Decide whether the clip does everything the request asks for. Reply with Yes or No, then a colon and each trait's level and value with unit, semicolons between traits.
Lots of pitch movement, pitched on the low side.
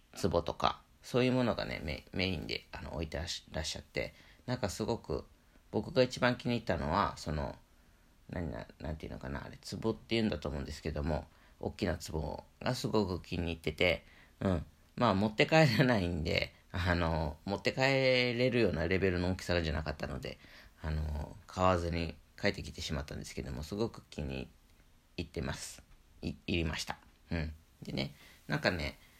Yes: wide, 5.7 semitones; very low, 85 Hz